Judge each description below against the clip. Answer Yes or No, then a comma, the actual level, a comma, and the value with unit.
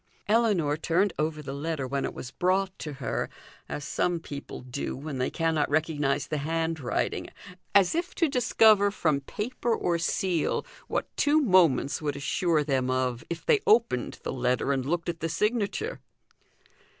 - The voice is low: No, medium, 160 Hz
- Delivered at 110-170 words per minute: Yes, average, 160 wpm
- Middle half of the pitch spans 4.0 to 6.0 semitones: Yes, wide, 5.6 semitones